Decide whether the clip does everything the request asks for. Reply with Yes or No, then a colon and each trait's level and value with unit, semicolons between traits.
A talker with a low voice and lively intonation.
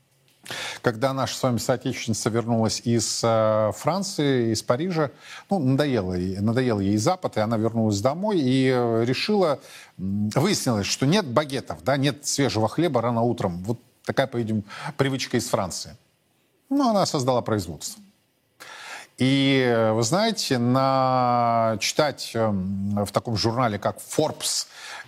No: low, 125 Hz; average, 3.4 semitones